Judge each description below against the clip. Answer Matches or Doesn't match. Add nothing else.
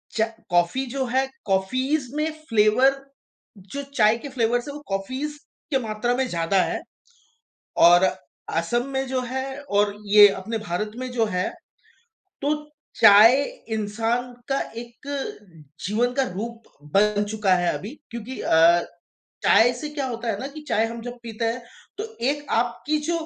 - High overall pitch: Matches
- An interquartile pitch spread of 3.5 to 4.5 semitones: Matches